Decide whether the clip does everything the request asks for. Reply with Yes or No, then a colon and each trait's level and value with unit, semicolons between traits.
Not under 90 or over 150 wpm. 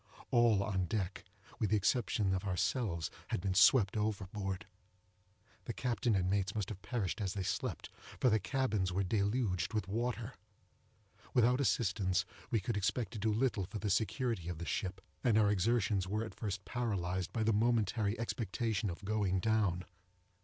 No: average, 165 wpm